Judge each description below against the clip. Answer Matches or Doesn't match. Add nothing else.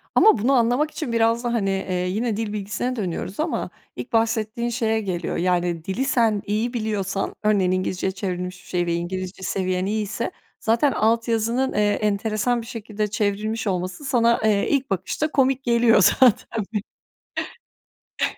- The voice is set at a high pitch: Matches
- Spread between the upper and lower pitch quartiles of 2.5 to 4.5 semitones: Matches